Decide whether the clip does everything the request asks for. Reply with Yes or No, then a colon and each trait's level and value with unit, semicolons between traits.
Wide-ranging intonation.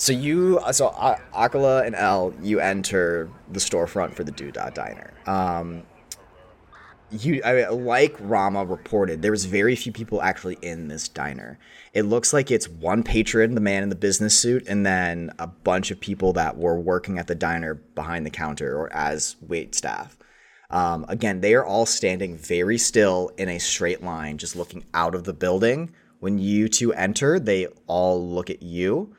No: average, 4.3 semitones